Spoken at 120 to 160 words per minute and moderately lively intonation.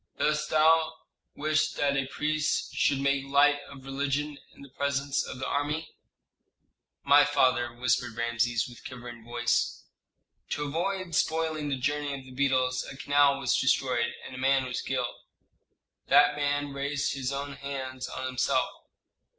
No: average, 150 wpm; narrow, 2.1 semitones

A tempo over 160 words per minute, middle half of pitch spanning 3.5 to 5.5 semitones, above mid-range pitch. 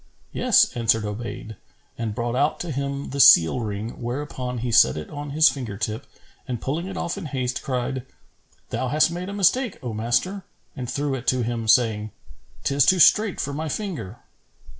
No: average, 185 wpm; average, 4.5 semitones; low, 130 Hz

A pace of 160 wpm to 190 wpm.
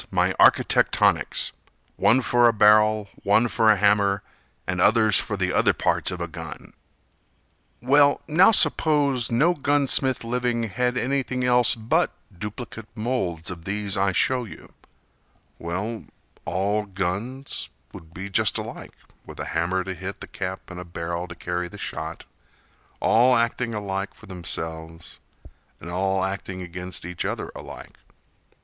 No: average, 140 wpm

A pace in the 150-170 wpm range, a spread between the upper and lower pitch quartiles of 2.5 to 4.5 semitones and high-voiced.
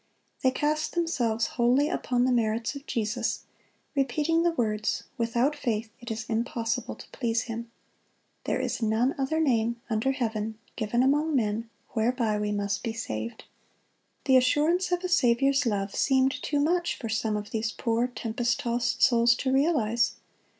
Yes: average, 155 wpm; average, 3.5 semitones; high, 240 Hz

